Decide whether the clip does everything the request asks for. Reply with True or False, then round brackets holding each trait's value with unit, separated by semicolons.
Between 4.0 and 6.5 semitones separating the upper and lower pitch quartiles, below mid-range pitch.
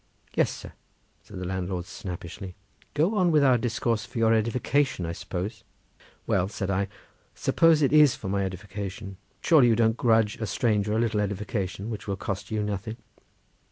False (3.5 semitones; 105 Hz)